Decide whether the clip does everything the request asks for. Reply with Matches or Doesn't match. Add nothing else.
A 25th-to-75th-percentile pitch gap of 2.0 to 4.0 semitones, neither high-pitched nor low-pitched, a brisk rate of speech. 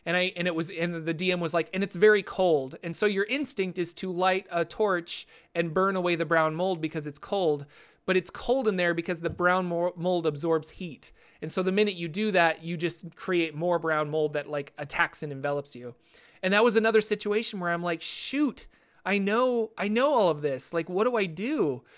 Matches